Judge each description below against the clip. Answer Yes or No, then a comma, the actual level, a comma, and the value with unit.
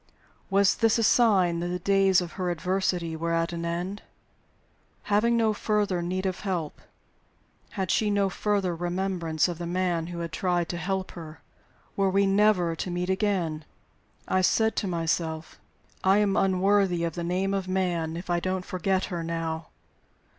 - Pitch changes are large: No, narrow, 2.4 semitones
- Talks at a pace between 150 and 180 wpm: Yes, average, 170 wpm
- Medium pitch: Yes, medium, 180 Hz